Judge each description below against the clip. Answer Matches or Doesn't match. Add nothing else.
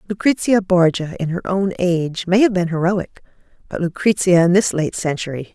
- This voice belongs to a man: Doesn't match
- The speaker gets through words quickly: Doesn't match